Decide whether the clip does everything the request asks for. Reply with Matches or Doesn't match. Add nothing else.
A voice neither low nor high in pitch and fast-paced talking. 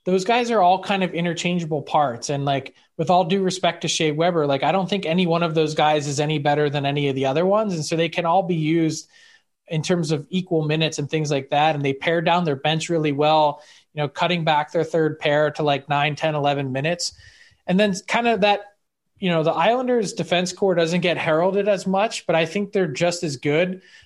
Matches